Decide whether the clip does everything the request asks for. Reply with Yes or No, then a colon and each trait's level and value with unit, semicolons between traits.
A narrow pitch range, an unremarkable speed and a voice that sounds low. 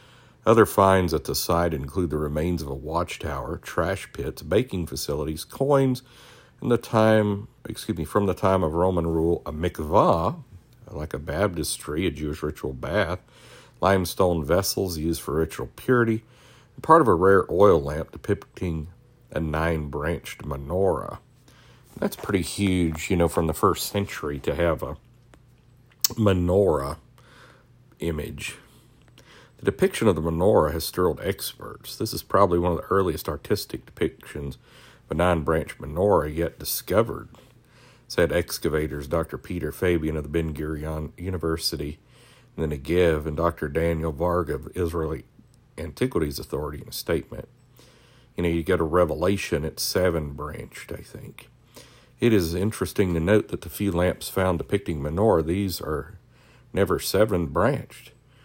No: average, 5.3 semitones; average, 145 wpm; very low, 90 Hz